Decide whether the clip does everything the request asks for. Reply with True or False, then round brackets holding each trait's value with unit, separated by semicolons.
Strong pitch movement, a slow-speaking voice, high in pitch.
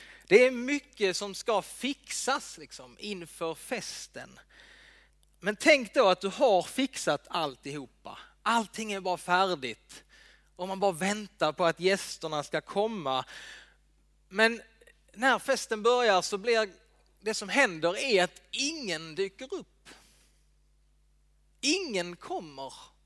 True (5.7 semitones; 120 wpm; 195 Hz)